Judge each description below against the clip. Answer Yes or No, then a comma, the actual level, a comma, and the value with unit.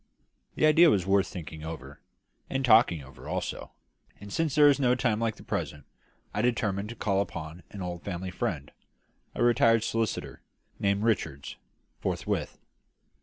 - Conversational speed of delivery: Yes, average, 155 wpm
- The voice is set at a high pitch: No, low, 100 Hz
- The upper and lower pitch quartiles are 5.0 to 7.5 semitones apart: Yes, wide, 5.5 semitones